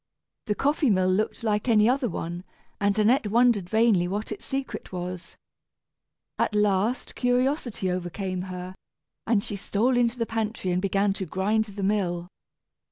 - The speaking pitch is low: No, high, 205 Hz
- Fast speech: No, average, 155 wpm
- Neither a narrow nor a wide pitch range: Yes, average, 3.7 semitones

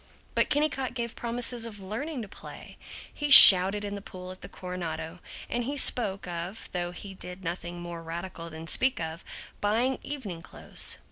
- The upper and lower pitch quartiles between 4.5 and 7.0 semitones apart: Yes, wide, 5.4 semitones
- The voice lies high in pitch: Yes, high, 195 Hz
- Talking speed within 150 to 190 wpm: Yes, average, 175 wpm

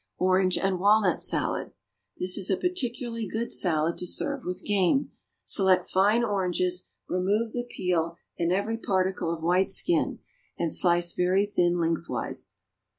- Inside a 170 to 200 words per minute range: No, average, 145 wpm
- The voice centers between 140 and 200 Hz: Yes, medium, 185 Hz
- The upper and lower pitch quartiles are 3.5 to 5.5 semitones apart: No, average, 2.9 semitones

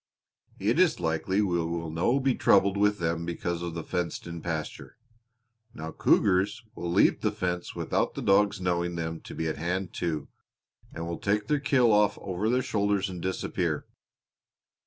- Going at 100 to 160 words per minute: No, average, 175 wpm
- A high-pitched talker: No, very low, 90 Hz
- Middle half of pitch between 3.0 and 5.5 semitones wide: Yes, average, 3.5 semitones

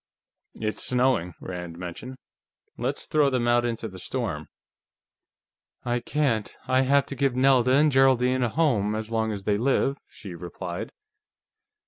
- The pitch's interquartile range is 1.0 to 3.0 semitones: No, average, 4.2 semitones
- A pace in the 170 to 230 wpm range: No, average, 145 wpm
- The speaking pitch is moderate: No, low, 120 Hz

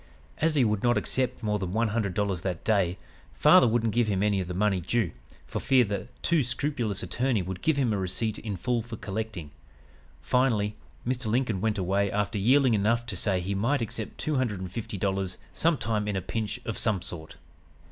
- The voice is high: No, low, 105 Hz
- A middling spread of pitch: Yes, average, 3.5 semitones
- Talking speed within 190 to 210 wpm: Yes, fast, 205 wpm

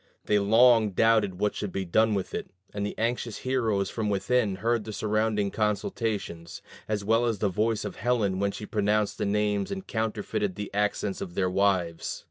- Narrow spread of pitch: Yes, narrow, 2.0 semitones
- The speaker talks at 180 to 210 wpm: Yes, average, 185 wpm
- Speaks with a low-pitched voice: Yes, low, 105 Hz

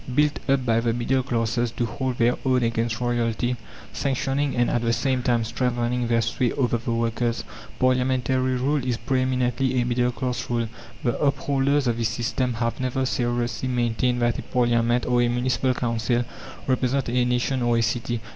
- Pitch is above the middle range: No, low, 120 Hz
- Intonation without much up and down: Yes, narrow, 1.5 semitones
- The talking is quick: No, average, 180 wpm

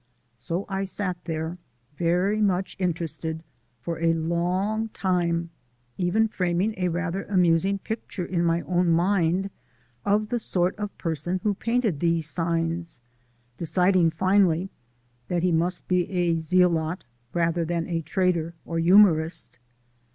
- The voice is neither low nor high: Yes, medium, 175 Hz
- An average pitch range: No, narrow, 2.3 semitones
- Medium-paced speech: No, slow, 130 wpm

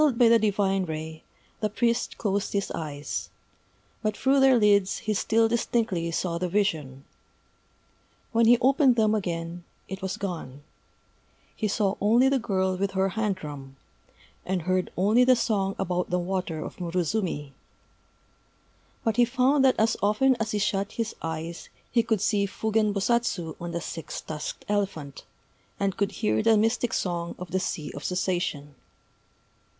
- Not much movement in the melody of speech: No, average, 4.3 semitones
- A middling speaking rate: Yes, average, 160 wpm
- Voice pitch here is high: Yes, high, 195 Hz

